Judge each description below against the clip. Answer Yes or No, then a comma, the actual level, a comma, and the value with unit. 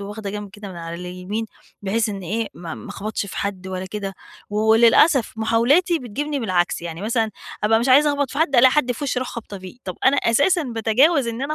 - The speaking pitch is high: Yes, high, 225 Hz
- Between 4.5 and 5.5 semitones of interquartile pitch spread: Yes, average, 4.8 semitones